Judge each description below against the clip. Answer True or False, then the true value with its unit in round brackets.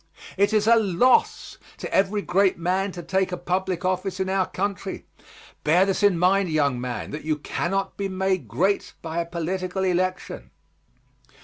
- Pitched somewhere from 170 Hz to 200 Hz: True (185 Hz)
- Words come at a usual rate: True (170 wpm)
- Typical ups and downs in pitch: False (2.1 semitones)